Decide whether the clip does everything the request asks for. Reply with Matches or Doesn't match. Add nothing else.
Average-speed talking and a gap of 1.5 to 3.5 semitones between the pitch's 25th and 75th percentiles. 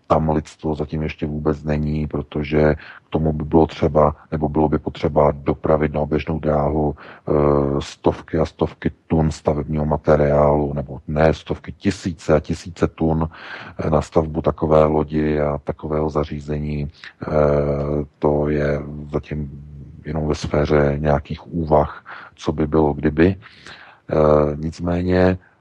Doesn't match